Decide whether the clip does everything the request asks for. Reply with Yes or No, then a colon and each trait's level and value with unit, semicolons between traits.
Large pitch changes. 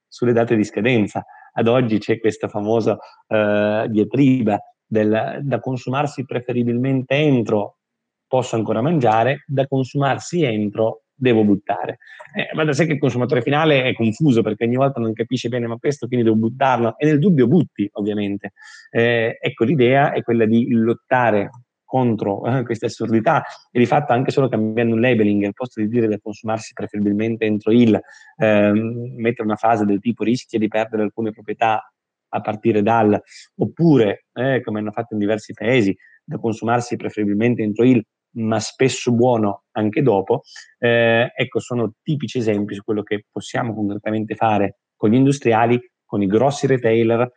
No: average, 2.8 semitones